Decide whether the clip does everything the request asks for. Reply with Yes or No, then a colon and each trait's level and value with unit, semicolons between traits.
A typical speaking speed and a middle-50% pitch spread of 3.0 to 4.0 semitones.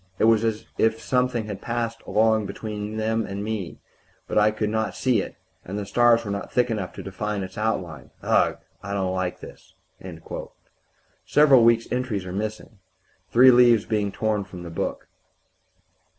No: average, 175 wpm; narrow, 2.4 semitones